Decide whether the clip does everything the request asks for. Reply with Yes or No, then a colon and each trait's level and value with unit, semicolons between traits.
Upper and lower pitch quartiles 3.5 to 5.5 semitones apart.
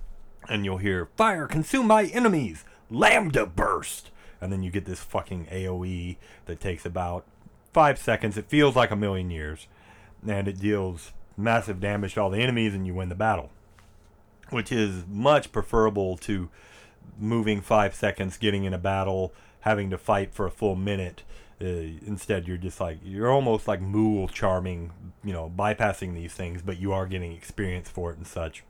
No: average, 2.8 semitones